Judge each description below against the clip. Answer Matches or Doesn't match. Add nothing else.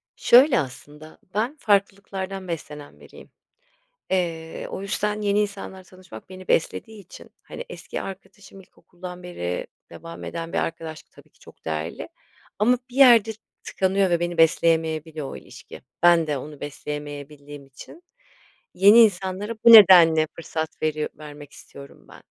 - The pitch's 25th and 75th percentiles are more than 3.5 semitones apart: Matches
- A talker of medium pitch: Matches